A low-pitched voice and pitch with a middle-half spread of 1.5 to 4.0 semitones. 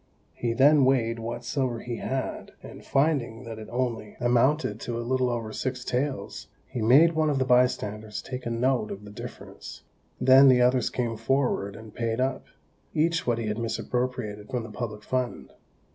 Yes: low, 125 Hz; narrow, 2.5 semitones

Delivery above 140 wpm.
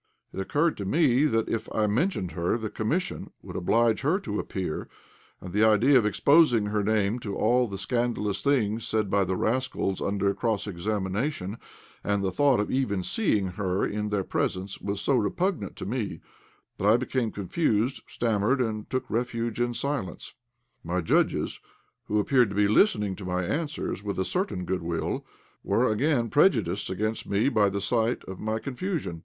Yes: average, 175 wpm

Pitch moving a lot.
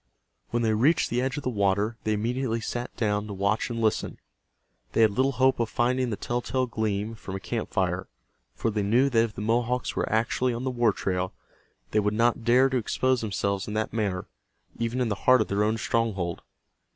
No: average, 2.9 semitones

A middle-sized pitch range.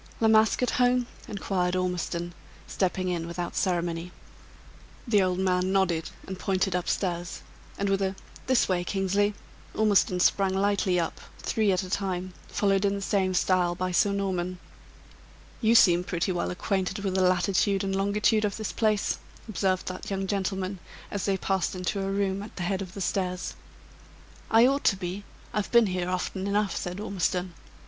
No: narrow, 1.8 semitones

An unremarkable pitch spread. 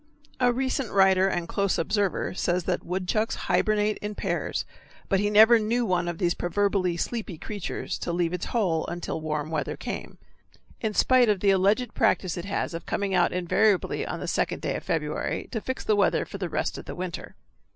Yes: average, 3.4 semitones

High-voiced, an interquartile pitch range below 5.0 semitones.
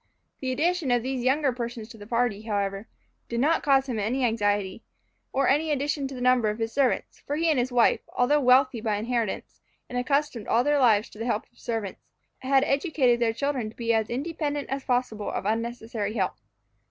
Yes: high, 245 Hz; average, 3.5 semitones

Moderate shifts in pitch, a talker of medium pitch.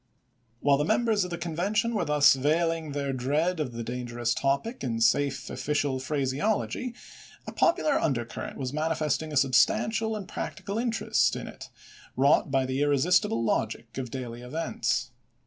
Yes: average, 5.0 semitones; medium, 145 Hz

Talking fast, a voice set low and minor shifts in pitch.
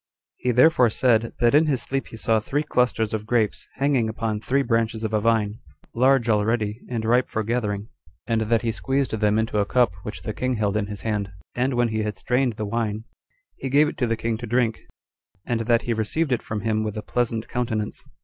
Yes: fast, 225 wpm; low, 115 Hz; narrow, 2.3 semitones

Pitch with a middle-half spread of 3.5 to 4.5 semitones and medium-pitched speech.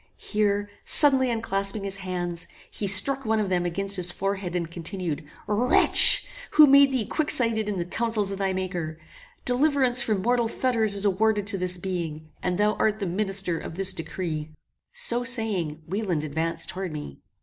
No: average, 4.0 semitones; high, 195 Hz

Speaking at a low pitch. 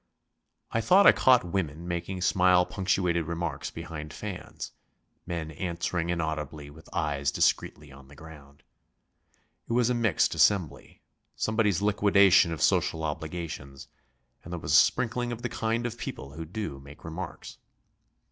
Yes: very low, 85 Hz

